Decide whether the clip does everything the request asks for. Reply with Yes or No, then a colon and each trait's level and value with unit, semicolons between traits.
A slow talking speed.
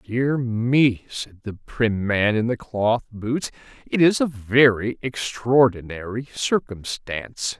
Yes: slow, 125 wpm